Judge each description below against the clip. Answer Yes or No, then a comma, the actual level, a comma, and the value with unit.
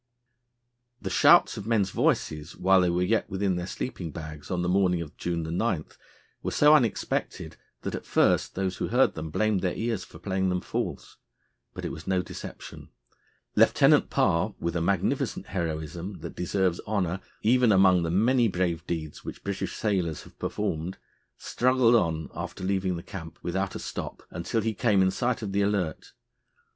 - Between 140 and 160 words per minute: No, average, 175 wpm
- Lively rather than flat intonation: No, average, 3.3 semitones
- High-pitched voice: No, very low, 95 Hz